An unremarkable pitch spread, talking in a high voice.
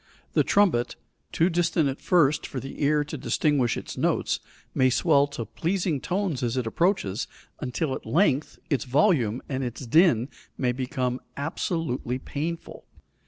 No: average, 4.8 semitones; medium, 140 Hz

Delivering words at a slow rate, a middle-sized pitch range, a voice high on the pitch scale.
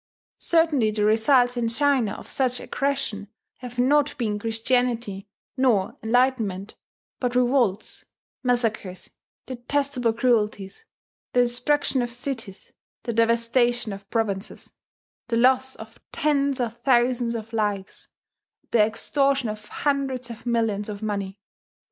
Yes: slow, 120 wpm; average, 3.0 semitones; high, 240 Hz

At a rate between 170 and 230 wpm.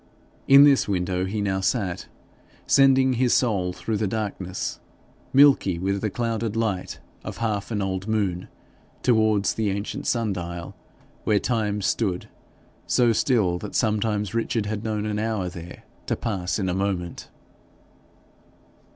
No: average, 140 wpm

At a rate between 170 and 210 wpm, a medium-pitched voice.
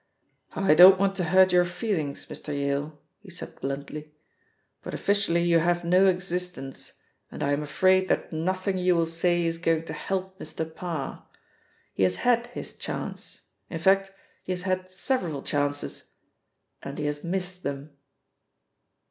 No: average, 155 wpm; medium, 175 Hz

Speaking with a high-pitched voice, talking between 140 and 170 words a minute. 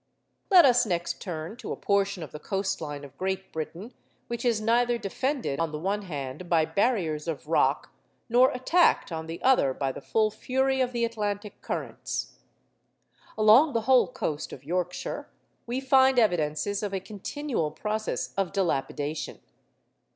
Yes: high, 200 Hz; average, 160 wpm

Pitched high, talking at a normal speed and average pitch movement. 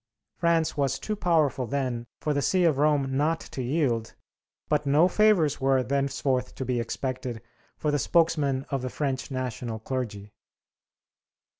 No: low, 135 Hz; average, 150 wpm; average, 3.1 semitones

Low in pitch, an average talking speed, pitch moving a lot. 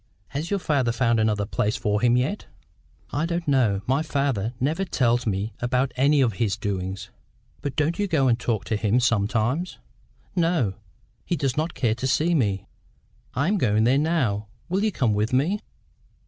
Yes: low, 125 Hz; average, 180 wpm; wide, 6.0 semitones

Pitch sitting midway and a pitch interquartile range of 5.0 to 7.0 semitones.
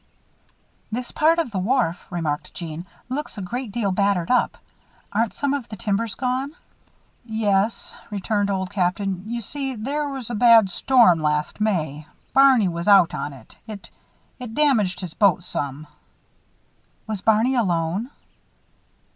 No: high, 210 Hz; wide, 5.4 semitones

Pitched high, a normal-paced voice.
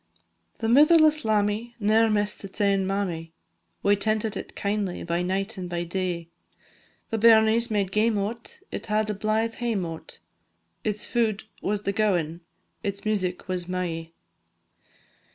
Yes: high, 205 Hz; average, 145 wpm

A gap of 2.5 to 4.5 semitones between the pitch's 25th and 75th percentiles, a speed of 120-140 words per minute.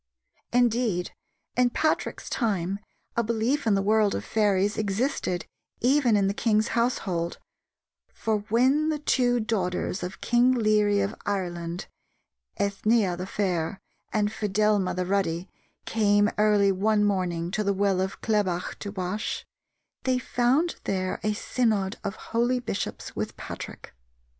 Yes: average, 3.4 semitones; slow, 135 wpm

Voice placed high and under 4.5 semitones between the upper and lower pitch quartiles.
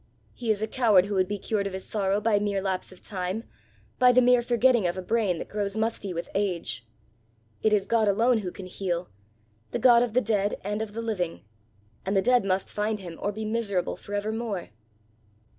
Yes: high, 205 Hz; average, 2.9 semitones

